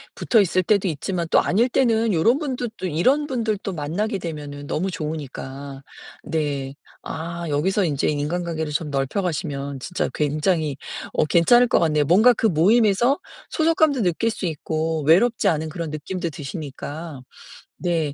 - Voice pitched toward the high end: No, medium, 170 Hz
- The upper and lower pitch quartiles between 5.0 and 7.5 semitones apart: Yes, wide, 5.6 semitones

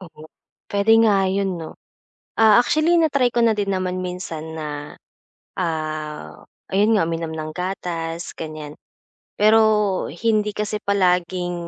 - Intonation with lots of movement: No, average, 4.3 semitones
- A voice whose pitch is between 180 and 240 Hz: Yes, medium, 185 Hz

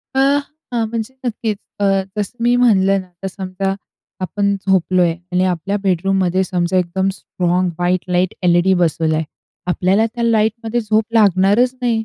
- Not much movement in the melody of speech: No, average, 3.4 semitones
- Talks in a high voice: Yes, high, 195 Hz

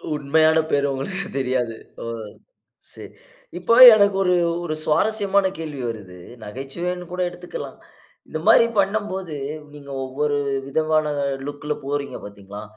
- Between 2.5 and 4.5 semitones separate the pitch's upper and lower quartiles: No, average, 5.0 semitones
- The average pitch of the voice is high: No, medium, 150 Hz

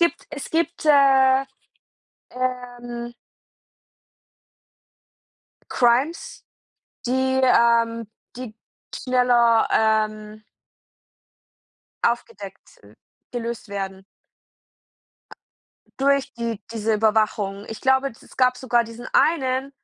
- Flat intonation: No, average, 3.0 semitones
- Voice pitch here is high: Yes, high, 240 Hz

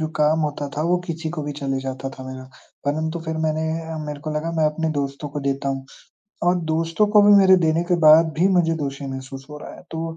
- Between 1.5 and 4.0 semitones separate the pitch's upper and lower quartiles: Yes, average, 2.7 semitones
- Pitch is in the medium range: Yes, medium, 155 Hz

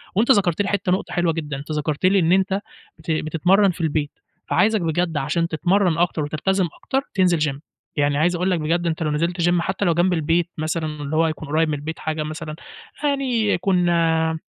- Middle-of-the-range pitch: Yes, medium, 170 Hz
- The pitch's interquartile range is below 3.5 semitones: Yes, average, 2.9 semitones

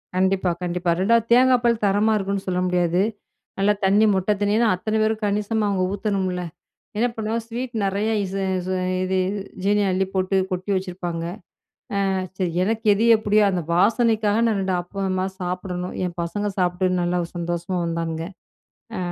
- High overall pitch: Yes, high, 195 Hz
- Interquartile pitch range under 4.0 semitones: Yes, average, 2.8 semitones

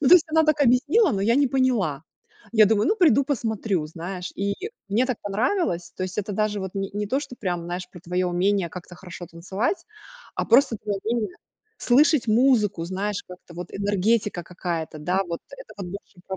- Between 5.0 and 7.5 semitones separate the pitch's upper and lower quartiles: Yes, wide, 5.4 semitones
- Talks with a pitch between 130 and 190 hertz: No, high, 205 Hz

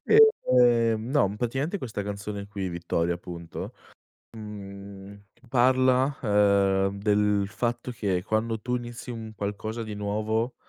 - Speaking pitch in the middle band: No, low, 105 Hz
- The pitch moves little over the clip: No, average, 3.1 semitones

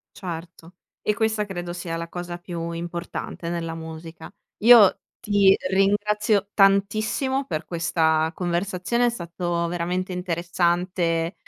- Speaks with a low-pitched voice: No, medium, 175 Hz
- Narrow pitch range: No, average, 3.0 semitones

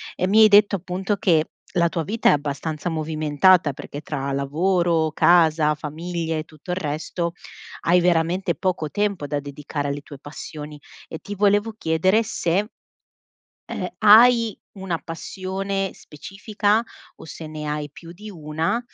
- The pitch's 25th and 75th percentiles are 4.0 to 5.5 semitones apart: Yes, average, 4.3 semitones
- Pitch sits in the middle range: Yes, medium, 170 Hz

